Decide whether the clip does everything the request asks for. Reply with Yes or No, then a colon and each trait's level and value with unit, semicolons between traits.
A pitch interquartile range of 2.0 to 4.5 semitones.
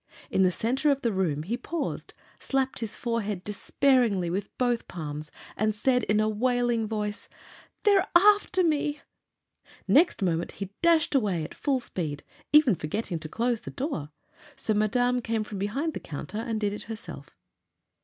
No: average, 5.2 semitones